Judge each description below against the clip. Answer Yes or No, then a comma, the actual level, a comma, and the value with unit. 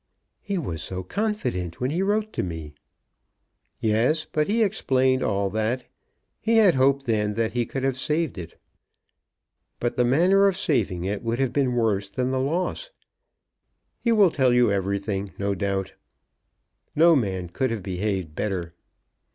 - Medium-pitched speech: No, low, 120 Hz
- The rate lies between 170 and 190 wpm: No, average, 160 wpm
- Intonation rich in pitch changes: Yes, wide, 7.6 semitones